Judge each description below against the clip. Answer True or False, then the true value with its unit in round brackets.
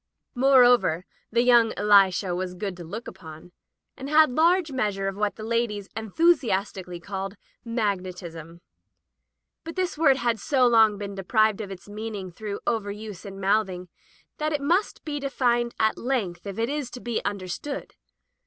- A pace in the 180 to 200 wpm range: False (165 wpm)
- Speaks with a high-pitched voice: True (215 Hz)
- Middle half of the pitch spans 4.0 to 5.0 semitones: True (4.4 semitones)